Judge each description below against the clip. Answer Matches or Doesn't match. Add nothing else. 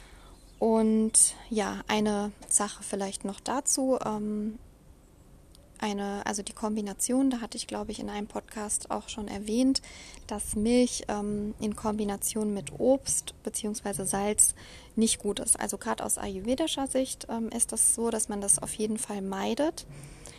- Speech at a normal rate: Matches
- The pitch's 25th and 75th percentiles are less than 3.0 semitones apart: Matches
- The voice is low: Doesn't match